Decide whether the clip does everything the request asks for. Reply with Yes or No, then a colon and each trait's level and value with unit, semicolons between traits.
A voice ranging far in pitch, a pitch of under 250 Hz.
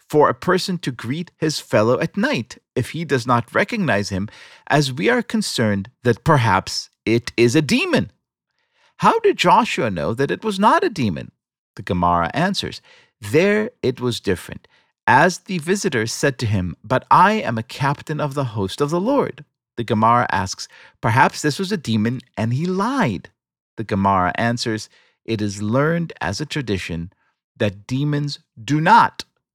Yes: wide, 8.3 semitones; medium, 140 Hz